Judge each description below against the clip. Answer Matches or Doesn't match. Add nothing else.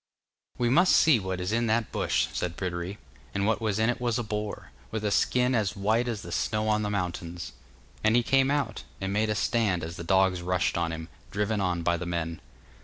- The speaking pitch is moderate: Doesn't match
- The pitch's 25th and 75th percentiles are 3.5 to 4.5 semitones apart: Matches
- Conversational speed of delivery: Doesn't match